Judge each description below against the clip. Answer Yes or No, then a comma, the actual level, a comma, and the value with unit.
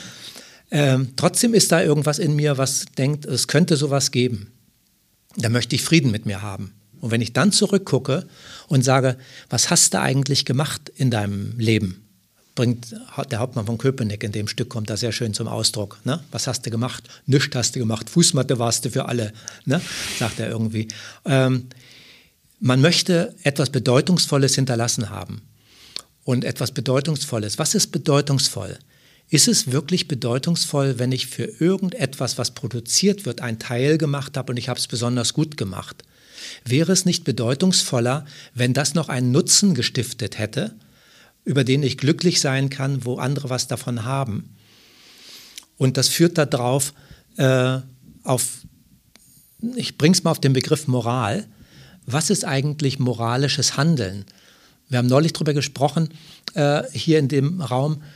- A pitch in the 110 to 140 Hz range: Yes, low, 135 Hz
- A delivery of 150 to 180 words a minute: Yes, average, 160 wpm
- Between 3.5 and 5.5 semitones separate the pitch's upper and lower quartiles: Yes, average, 3.8 semitones